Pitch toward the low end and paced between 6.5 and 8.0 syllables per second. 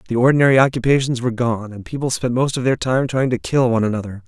Yes: low, 125 Hz; 6.9 syllables/s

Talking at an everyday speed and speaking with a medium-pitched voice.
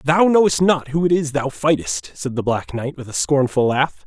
No: fast, 235 wpm; medium, 145 Hz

